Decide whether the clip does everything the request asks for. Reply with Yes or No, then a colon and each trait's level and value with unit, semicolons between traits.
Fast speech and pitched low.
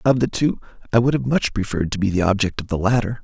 Yes: fast, 280 wpm; low, 110 Hz